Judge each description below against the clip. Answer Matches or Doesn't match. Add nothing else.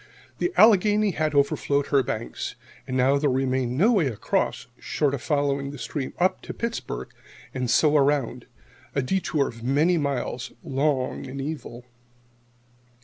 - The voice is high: Doesn't match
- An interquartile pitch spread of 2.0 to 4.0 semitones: Matches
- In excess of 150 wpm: Doesn't match